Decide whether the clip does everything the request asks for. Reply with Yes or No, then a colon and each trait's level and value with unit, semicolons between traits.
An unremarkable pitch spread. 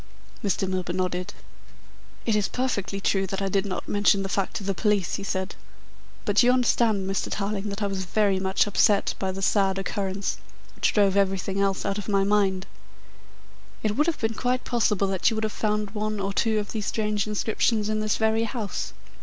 No: narrow, 1.7 semitones